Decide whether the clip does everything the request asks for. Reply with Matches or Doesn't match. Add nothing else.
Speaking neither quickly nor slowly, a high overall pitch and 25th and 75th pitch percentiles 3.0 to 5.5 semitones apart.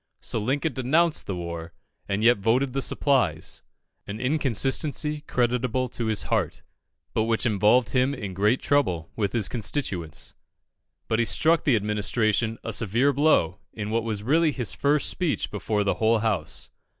Doesn't match